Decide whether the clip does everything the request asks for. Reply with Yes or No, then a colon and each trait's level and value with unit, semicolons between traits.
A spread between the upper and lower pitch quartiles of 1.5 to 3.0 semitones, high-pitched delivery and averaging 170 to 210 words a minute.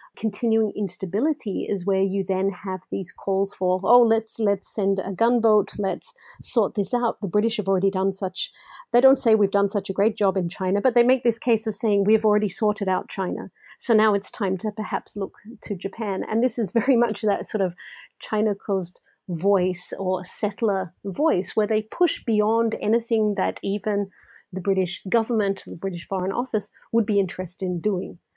Yes: narrow, 2.6 semitones; high, 205 Hz; average, 190 wpm